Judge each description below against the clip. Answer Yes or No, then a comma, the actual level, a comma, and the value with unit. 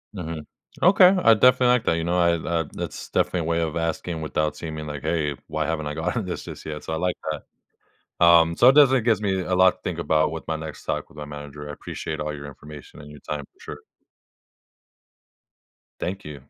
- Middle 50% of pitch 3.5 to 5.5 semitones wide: No, average, 3.1 semitones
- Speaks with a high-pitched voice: No, very low, 80 Hz